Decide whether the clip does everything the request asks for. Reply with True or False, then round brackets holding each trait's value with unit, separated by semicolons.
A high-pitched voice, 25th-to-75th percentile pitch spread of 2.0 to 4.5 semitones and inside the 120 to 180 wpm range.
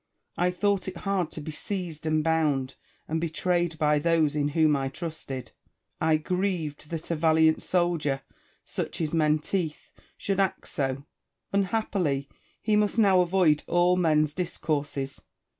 False (160 Hz; 3.1 semitones; 140 wpm)